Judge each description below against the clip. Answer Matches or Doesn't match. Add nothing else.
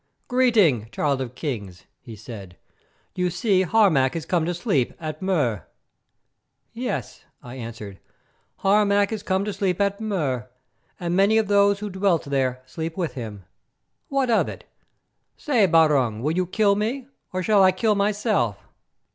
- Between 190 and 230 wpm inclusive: Doesn't match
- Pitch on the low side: Doesn't match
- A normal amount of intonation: Doesn't match